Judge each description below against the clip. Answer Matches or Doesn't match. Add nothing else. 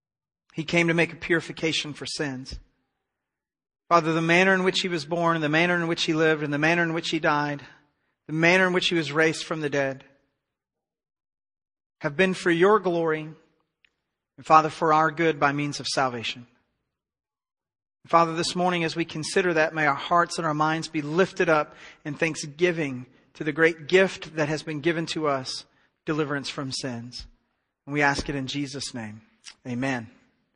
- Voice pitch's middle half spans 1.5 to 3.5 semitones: Matches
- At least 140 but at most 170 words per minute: Doesn't match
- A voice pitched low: Doesn't match